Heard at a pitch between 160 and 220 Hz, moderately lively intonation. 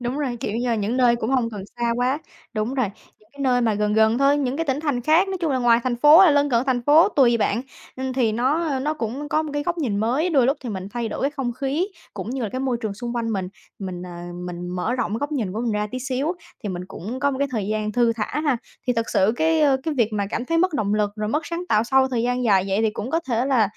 No: high, 245 Hz; average, 4.5 semitones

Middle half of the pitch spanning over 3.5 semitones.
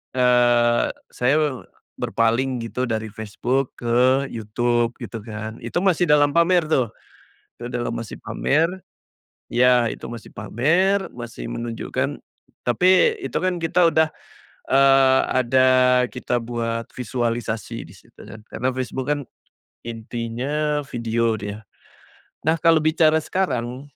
Yes: average, 4.1 semitones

